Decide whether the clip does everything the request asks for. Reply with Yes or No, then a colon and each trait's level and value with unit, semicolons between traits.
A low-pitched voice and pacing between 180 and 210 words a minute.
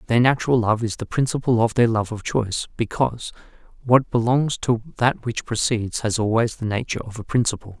Yes: low, 115 Hz; average, 190 wpm